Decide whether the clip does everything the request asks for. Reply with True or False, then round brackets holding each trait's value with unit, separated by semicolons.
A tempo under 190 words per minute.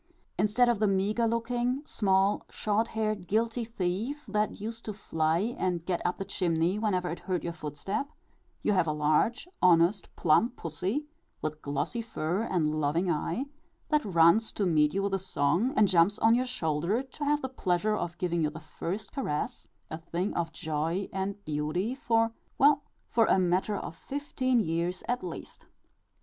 True (175 wpm)